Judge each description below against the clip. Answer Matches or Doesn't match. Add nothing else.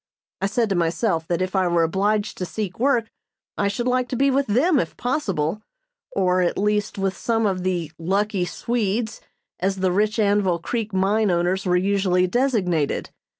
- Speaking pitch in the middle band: Doesn't match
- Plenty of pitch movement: Doesn't match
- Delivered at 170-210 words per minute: Matches